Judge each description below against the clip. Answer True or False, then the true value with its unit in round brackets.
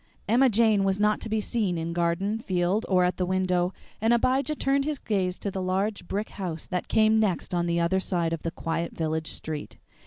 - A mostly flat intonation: False (4.1 semitones)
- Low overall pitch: False (190 Hz)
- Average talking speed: False (215 wpm)